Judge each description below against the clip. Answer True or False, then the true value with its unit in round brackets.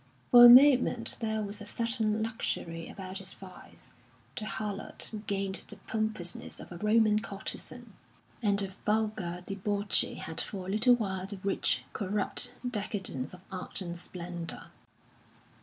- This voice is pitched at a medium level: False (205 Hz)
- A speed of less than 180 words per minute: True (140 wpm)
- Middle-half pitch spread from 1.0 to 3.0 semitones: True (2.6 semitones)